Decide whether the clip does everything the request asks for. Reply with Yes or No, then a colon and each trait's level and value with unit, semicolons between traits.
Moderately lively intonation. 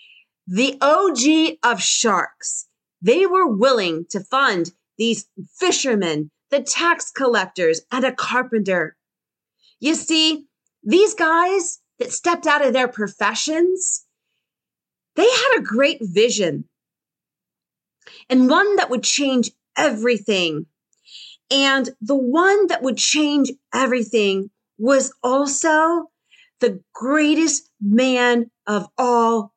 No: wide, 6.0 semitones